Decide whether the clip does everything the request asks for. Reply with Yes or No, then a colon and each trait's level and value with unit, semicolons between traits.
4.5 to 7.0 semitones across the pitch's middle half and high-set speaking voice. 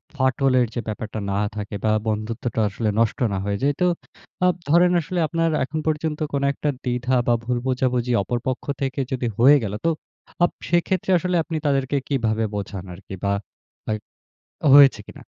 No: average, 5.1 semitones; low, 130 Hz